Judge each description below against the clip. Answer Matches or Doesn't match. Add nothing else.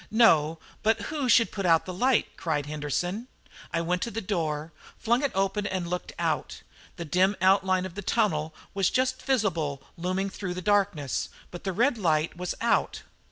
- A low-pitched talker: Doesn't match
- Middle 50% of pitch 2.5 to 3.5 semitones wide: Doesn't match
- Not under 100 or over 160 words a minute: Doesn't match